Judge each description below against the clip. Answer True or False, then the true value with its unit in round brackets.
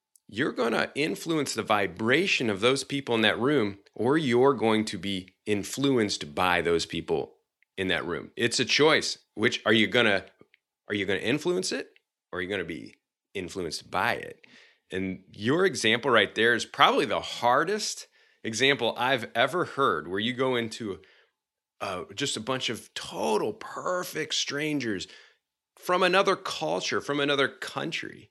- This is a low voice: True (125 Hz)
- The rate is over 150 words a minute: True (165 wpm)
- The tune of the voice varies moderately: False (5.9 semitones)